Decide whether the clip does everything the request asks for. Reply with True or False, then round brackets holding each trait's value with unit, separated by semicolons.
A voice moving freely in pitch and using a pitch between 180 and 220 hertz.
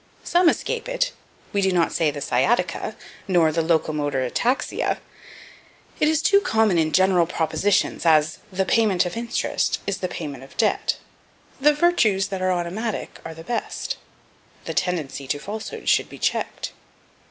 True (6.0 semitones; 185 Hz)